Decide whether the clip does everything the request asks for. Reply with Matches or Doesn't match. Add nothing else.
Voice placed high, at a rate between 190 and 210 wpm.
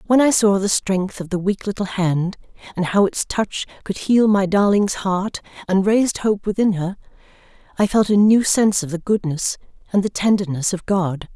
Matches